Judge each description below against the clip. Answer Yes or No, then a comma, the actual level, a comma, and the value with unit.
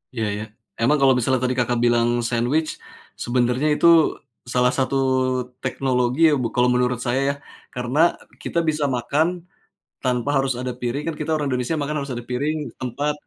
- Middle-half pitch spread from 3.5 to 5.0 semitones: No, average, 2.7 semitones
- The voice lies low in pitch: Yes, low, 125 Hz